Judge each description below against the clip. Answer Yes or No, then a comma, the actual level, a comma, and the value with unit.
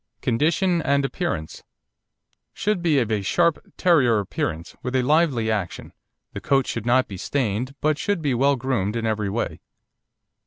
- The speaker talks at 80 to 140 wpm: No, average, 160 wpm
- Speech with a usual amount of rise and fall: No, wide, 5.7 semitones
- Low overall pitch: Yes, low, 130 Hz